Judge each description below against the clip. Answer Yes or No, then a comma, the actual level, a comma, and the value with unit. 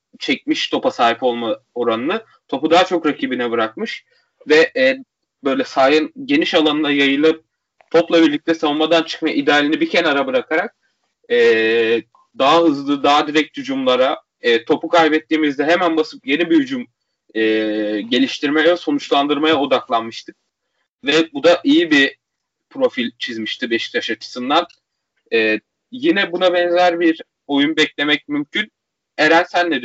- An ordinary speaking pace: Yes, average, 125 wpm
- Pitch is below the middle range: No, medium, 165 Hz